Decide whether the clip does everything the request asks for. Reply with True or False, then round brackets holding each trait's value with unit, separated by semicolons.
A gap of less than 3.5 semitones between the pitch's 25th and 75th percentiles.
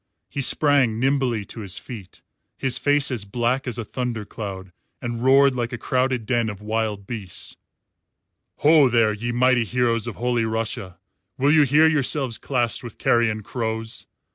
True (2.8 semitones)